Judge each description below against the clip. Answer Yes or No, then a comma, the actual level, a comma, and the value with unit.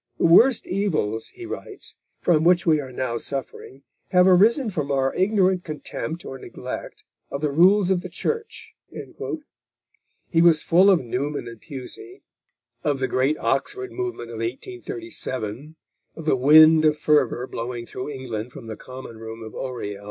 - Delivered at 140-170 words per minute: Yes, average, 160 wpm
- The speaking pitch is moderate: Yes, medium, 150 Hz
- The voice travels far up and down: Yes, wide, 6.4 semitones